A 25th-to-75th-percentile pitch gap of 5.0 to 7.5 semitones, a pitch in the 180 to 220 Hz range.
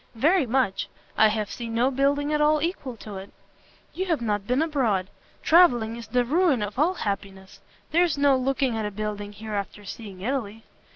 No: wide, 5.6 semitones; high, 240 Hz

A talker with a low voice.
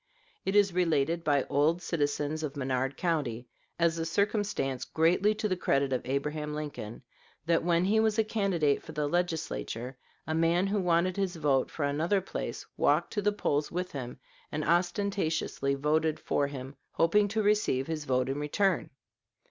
No: medium, 160 Hz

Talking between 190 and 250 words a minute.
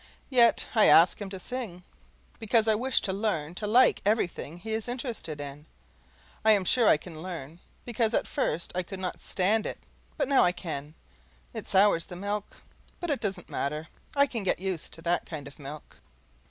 Yes: average, 195 wpm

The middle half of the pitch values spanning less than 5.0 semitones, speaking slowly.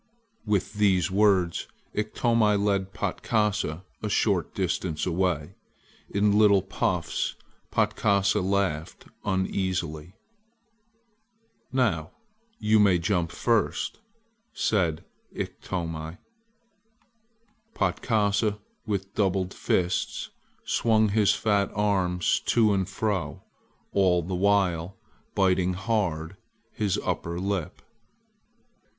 Yes: average, 2.7 semitones; slow, 85 wpm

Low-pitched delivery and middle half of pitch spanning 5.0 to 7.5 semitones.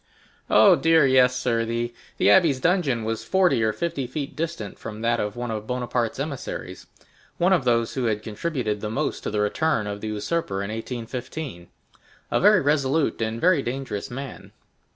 Yes: low, 125 Hz; average, 5.3 semitones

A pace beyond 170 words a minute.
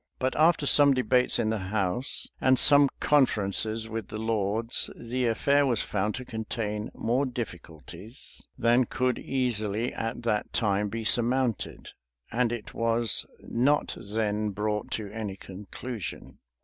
No: slow, 135 wpm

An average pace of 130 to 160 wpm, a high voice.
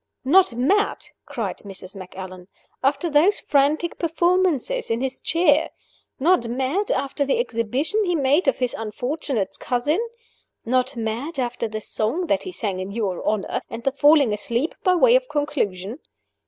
Yes: average, 155 wpm; very high, 270 Hz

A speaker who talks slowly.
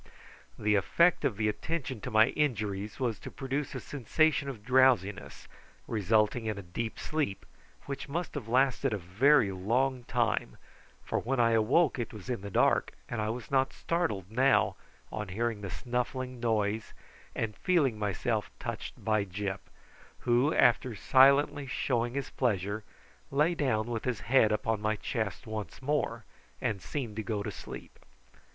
No: average, 160 wpm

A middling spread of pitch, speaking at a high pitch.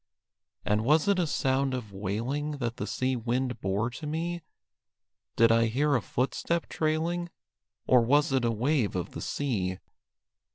No: average, 4.6 semitones; low, 130 Hz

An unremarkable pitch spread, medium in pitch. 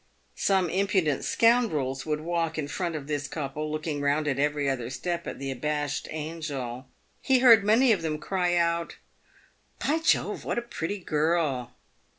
Yes: average, 3.8 semitones; medium, 155 Hz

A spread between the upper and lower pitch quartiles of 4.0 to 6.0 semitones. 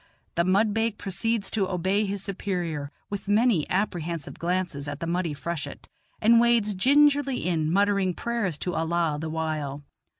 Yes: average, 4.5 semitones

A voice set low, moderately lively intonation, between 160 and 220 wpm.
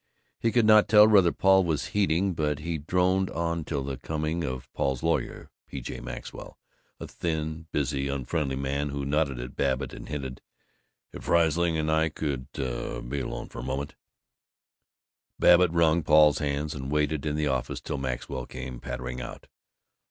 Yes: very low, 75 Hz; average, 3.6 semitones; average, 170 wpm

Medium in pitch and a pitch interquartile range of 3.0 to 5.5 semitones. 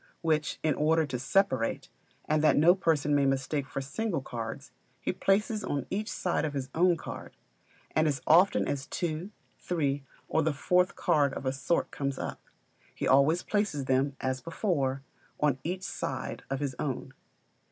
Yes: medium, 150 Hz; average, 4.2 semitones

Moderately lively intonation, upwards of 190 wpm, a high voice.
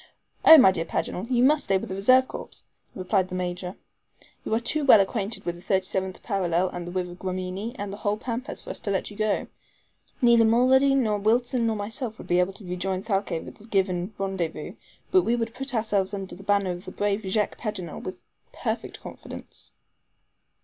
Yes: average, 3.8 semitones; average, 200 wpm; high, 200 Hz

